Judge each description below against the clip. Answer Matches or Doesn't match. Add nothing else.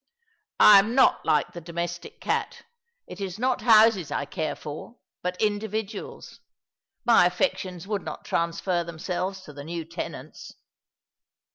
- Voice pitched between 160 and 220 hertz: Matches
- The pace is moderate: Matches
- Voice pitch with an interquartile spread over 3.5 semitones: Matches